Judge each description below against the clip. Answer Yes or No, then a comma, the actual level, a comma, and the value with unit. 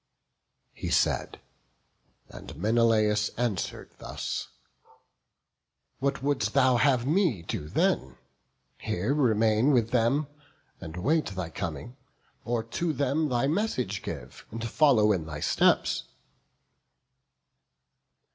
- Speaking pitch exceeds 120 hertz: No, low, 115 Hz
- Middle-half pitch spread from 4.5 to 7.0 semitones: Yes, wide, 5.4 semitones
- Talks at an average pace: No, slow, 105 wpm